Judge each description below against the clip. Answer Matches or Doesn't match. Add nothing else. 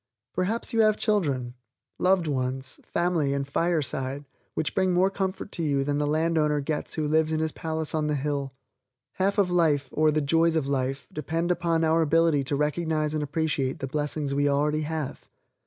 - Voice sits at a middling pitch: Matches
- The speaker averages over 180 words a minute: Matches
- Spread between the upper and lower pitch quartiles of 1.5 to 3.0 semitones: Matches